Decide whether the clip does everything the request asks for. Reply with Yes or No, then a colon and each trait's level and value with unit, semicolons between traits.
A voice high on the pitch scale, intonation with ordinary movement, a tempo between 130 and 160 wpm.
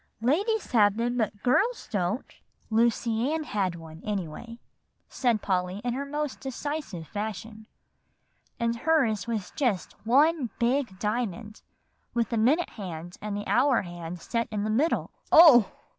Yes: high, 230 Hz; average, 4.4 semitones; average, 145 wpm